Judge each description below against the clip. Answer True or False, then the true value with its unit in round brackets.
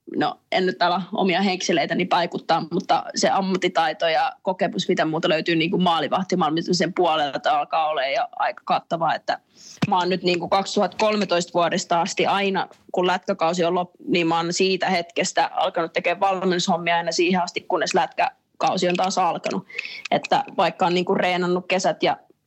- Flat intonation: True (1.9 semitones)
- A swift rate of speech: True (165 wpm)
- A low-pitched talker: False (180 Hz)